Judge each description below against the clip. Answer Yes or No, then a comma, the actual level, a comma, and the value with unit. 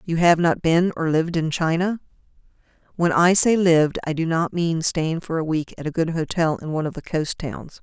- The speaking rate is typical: No, fast, 230 wpm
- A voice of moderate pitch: Yes, medium, 165 Hz